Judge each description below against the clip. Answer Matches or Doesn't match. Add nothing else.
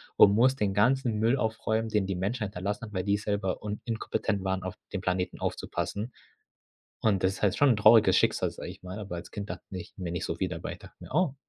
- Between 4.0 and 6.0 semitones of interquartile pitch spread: Doesn't match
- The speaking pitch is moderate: Doesn't match